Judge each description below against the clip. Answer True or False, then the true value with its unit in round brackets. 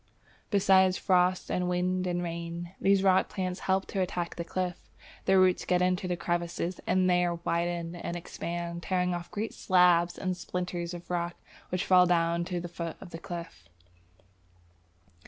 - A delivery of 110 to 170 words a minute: True (165 wpm)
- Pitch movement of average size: False (1.2 semitones)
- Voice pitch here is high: False (180 Hz)